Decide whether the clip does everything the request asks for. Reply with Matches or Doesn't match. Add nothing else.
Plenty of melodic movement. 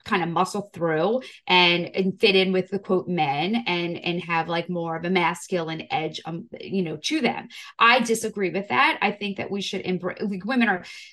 Doesn't match